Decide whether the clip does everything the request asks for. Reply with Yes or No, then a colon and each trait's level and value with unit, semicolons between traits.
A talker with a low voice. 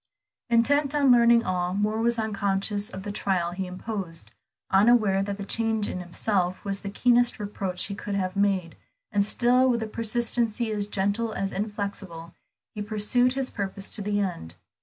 No: high, 205 Hz